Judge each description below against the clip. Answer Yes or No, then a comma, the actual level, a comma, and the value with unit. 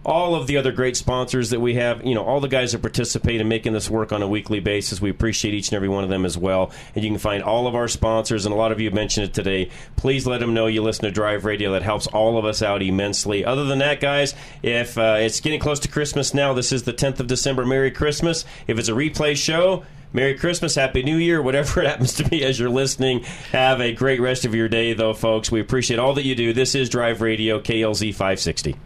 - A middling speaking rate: No, fast, 260 wpm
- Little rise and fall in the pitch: No, average, 3.8 semitones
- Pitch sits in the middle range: No, low, 120 Hz